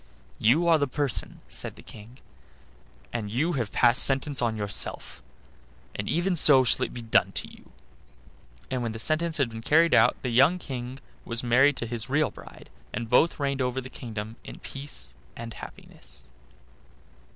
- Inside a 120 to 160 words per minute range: No, average, 175 wpm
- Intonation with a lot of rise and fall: No, average, 4.0 semitones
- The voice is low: Yes, low, 125 Hz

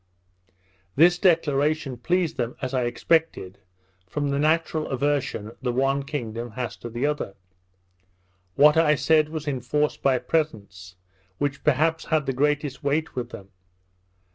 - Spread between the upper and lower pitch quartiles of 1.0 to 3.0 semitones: No, average, 3.8 semitones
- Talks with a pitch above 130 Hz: Yes, medium, 140 Hz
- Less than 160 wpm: Yes, average, 140 wpm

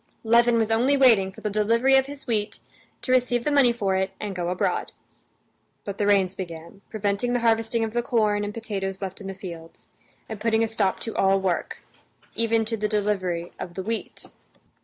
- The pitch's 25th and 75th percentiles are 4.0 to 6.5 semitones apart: No, average, 3.2 semitones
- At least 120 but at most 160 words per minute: No, average, 200 wpm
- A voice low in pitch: No, high, 210 Hz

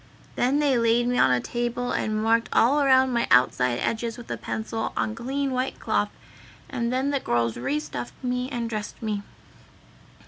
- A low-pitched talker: No, high, 235 Hz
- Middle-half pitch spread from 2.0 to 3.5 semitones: Yes, average, 3.0 semitones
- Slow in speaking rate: No, average, 180 wpm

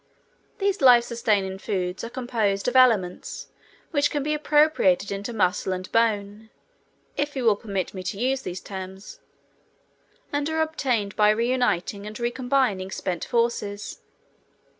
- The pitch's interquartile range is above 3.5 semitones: Yes, average, 4.7 semitones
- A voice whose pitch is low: No, high, 220 Hz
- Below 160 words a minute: Yes, average, 140 wpm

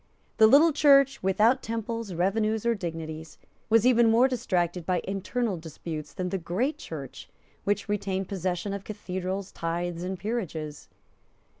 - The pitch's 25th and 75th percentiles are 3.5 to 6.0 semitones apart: Yes, average, 4.6 semitones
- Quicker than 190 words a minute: No, average, 140 wpm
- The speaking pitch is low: No, high, 195 Hz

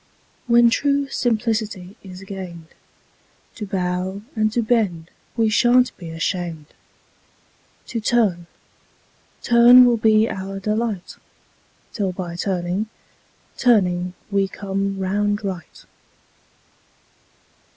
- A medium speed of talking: No, slow, 100 wpm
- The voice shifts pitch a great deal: No, average, 3.8 semitones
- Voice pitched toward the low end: No, high, 200 Hz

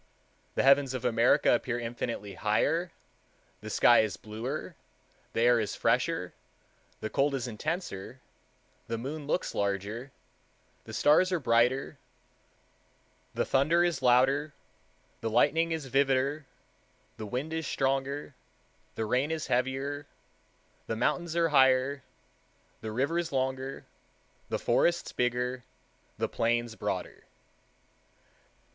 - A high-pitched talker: No, low, 130 Hz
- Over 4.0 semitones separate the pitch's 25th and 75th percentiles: No, average, 3.7 semitones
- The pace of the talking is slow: Yes, slow, 115 wpm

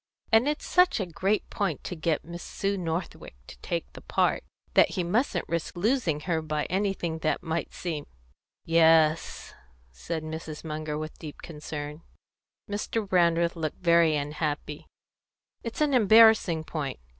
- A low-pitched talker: No, medium, 165 Hz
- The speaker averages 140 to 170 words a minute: Yes, average, 150 wpm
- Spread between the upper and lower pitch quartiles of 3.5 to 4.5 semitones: Yes, average, 3.8 semitones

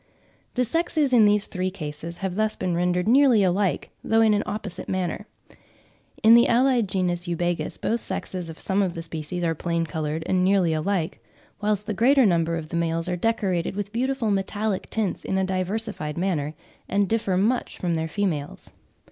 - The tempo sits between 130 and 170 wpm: No, average, 180 wpm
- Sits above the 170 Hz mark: Yes, high, 190 Hz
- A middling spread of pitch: Yes, average, 4.1 semitones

